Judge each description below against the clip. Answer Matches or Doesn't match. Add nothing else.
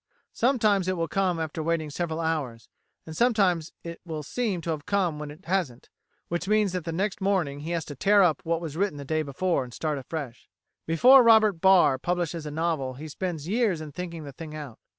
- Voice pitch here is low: Doesn't match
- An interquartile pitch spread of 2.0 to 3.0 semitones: Doesn't match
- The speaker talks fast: Matches